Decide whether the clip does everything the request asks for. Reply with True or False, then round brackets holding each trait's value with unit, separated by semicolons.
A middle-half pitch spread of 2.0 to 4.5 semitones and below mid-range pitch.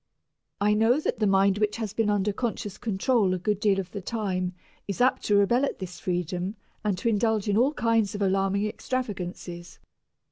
False (2.7 semitones; 205 Hz)